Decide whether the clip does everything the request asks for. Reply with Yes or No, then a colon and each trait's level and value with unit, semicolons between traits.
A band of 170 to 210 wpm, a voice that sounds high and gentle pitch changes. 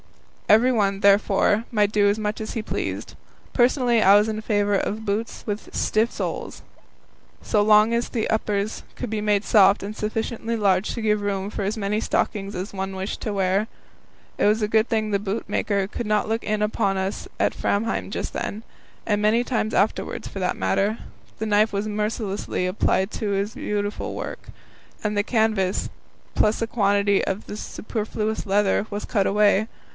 Yes: average, 180 wpm; high, 210 Hz; narrow, 1.5 semitones